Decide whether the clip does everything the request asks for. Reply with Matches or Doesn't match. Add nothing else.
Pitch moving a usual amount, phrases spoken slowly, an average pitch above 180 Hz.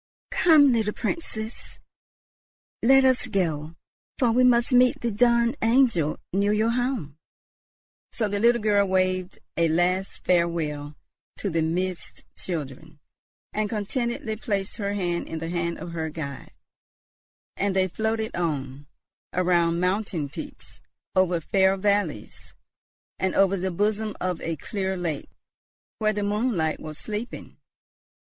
Matches